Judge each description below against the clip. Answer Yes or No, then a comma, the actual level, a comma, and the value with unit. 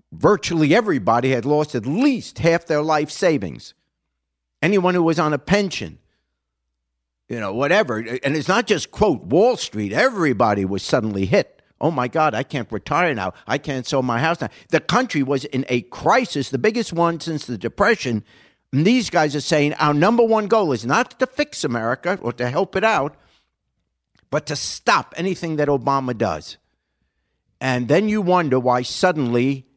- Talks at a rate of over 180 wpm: No, average, 175 wpm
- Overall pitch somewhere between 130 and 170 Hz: Yes, medium, 140 Hz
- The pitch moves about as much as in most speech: No, wide, 6.1 semitones